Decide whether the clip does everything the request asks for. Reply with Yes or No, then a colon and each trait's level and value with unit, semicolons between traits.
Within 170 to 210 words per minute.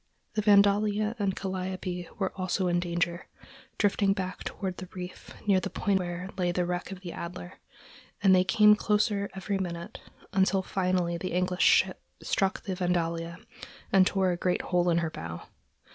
Yes: average, 175 wpm